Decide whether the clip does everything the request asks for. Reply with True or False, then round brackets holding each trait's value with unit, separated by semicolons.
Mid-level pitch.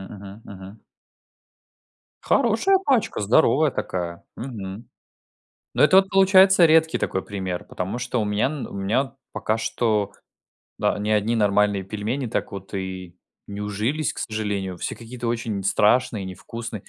False (110 Hz)